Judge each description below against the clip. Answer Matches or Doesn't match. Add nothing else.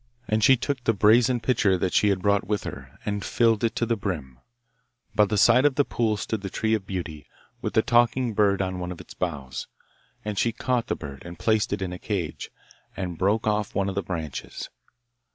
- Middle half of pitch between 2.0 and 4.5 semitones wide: Matches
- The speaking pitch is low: Matches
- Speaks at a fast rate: Matches